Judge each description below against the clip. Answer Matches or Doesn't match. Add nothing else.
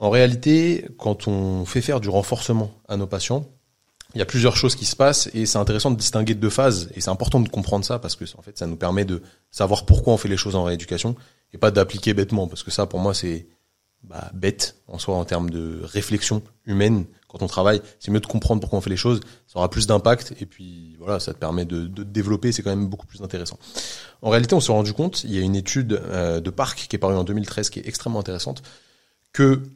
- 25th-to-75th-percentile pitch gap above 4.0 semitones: Doesn't match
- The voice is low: Matches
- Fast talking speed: Matches